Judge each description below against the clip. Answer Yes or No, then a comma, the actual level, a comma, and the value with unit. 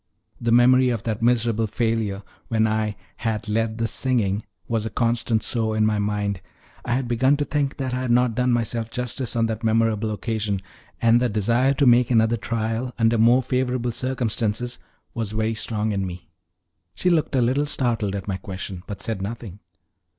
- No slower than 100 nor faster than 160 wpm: No, average, 185 wpm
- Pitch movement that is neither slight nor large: No, narrow, 2.3 semitones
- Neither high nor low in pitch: No, low, 115 Hz